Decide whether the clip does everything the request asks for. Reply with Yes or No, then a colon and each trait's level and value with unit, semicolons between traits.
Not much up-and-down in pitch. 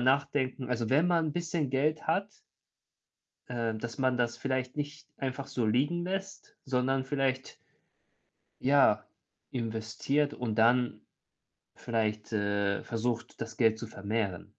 No: average, 3.9 semitones